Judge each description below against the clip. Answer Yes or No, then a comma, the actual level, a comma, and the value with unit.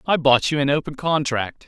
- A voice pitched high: No, medium, 145 Hz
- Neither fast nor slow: No, fast, 215 wpm